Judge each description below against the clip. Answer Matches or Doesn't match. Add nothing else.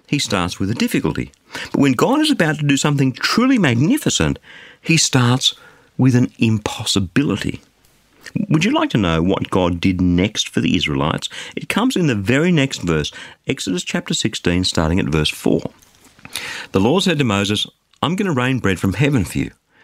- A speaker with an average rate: Matches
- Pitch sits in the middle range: Doesn't match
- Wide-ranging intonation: Matches